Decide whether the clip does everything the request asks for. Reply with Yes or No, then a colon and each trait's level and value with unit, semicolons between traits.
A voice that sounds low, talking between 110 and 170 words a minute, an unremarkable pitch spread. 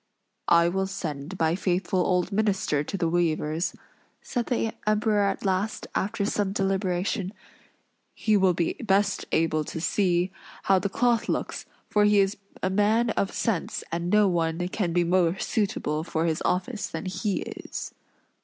No: high, 190 Hz; average, 160 wpm; average, 3.2 semitones